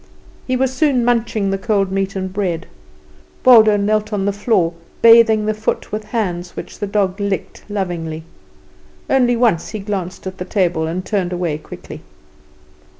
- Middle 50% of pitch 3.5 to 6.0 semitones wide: No, average, 3.1 semitones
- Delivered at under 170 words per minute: Yes, average, 160 wpm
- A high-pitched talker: Yes, high, 200 Hz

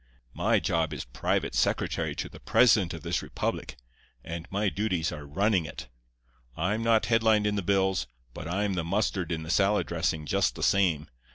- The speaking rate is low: No, average, 180 wpm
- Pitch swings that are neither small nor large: Yes, average, 4.4 semitones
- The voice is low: Yes, very low, 90 Hz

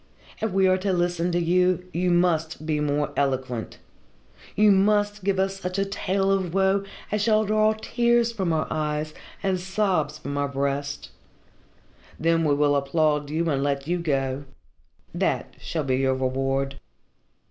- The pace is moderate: Yes, average, 160 wpm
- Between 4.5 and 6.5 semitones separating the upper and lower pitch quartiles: Yes, average, 5.1 semitones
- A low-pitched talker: No, medium, 170 Hz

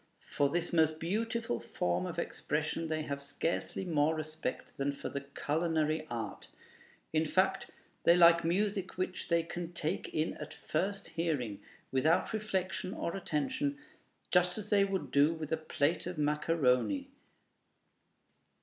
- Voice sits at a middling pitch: Yes, medium, 165 Hz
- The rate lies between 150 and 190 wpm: No, average, 140 wpm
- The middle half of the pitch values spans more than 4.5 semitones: No, average, 3.6 semitones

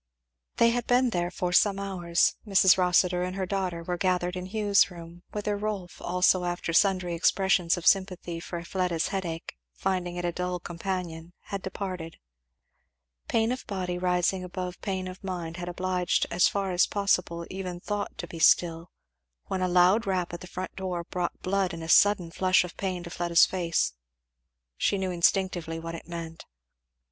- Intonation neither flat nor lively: No, narrow, 1.7 semitones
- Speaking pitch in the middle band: Yes, medium, 180 Hz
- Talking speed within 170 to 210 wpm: Yes, average, 175 wpm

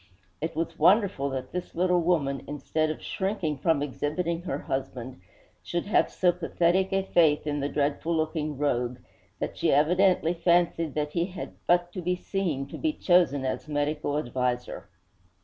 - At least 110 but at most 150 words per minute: No, average, 165 wpm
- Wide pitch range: No, average, 3.6 semitones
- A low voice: No, medium, 160 Hz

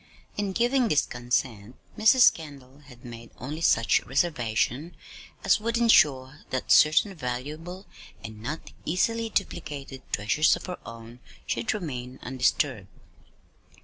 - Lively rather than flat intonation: Yes, wide, 6.6 semitones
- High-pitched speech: No, medium, 140 Hz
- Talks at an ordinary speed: No, slow, 120 wpm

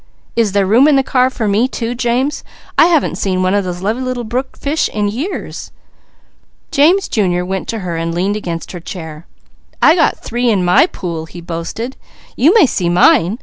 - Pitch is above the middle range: Yes, high, 215 Hz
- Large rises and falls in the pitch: Yes, wide, 6.2 semitones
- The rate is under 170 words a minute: No, average, 185 wpm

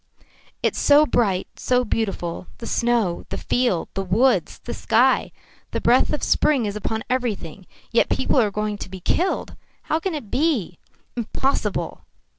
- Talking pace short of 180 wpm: Yes, average, 155 wpm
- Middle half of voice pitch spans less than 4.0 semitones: No, average, 4.8 semitones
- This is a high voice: Yes, high, 230 Hz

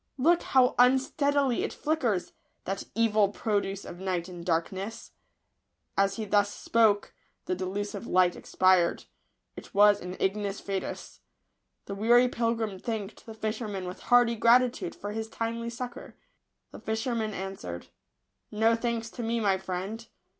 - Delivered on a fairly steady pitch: No, average, 3.3 semitones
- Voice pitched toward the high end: Yes, high, 215 Hz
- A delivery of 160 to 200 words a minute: No, average, 145 wpm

